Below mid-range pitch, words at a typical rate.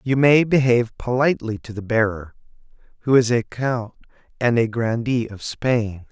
Yes: low, 120 Hz; average, 155 wpm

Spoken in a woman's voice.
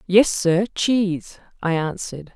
Yes: female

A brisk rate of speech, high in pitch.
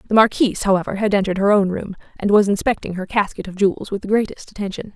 Yes: fast, 230 wpm; high, 200 Hz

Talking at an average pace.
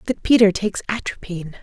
Yes: average, 150 wpm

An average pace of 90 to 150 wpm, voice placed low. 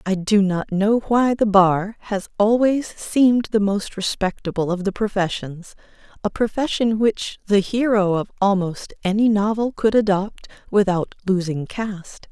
No: average, 145 wpm; high, 205 Hz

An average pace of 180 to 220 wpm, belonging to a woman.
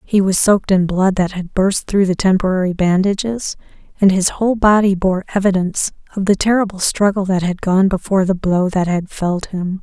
Yes: average, 195 wpm; female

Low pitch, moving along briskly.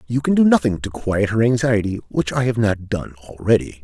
Yes: low, 105 Hz; fast, 220 wpm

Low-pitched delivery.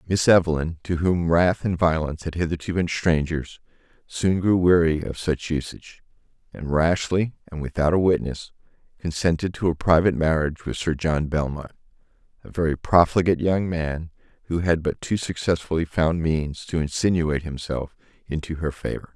Yes: very low, 85 Hz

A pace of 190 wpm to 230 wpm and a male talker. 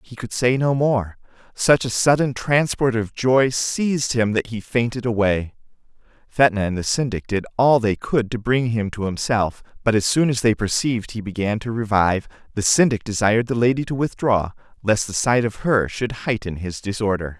Yes: average, 195 wpm; male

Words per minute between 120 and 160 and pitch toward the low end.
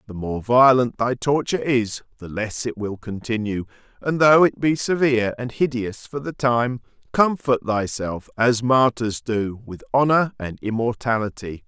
Yes: average, 155 wpm; low, 120 Hz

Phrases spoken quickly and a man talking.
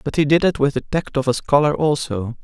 Yes: fast, 270 wpm; male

